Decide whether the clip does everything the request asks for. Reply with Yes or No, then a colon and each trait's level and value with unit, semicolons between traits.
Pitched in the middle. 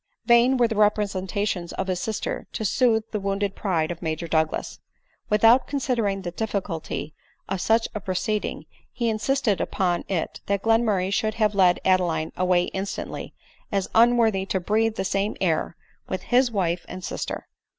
No: high, 200 Hz